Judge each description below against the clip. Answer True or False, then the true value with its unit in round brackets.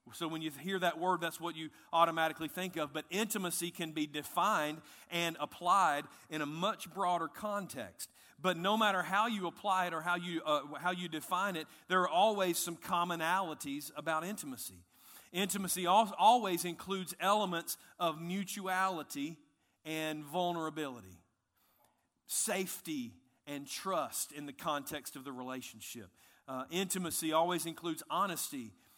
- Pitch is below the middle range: False (170 Hz)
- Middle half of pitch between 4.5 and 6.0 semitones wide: False (3.5 semitones)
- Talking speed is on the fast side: False (140 wpm)